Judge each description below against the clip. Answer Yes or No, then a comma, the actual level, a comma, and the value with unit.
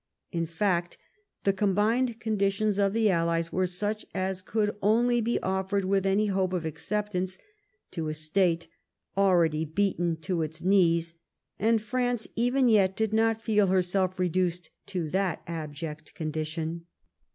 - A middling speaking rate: Yes, average, 150 wpm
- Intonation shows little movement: No, average, 3.8 semitones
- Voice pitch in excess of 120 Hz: Yes, high, 190 Hz